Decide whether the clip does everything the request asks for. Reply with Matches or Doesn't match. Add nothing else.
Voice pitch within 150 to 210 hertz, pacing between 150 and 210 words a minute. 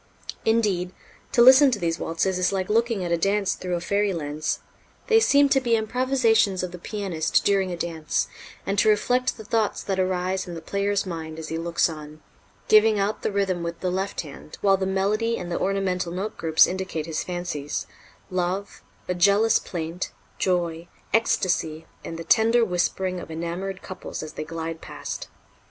Matches